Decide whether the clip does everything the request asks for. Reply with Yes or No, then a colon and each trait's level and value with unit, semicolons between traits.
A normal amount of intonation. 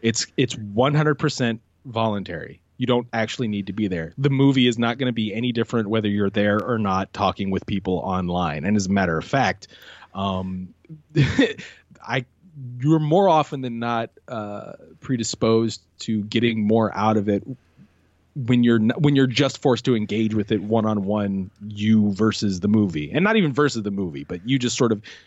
Yes: average, 3.9 semitones